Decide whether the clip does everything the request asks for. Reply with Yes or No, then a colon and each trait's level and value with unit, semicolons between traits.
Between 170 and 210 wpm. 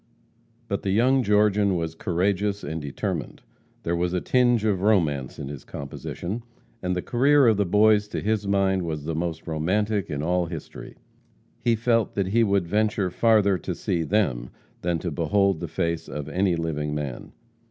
Yes: average, 175 wpm